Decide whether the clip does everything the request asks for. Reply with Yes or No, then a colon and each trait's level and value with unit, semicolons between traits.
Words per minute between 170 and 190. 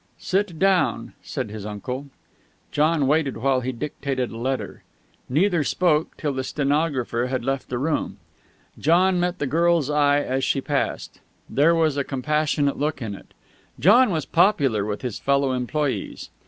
No: average, 155 wpm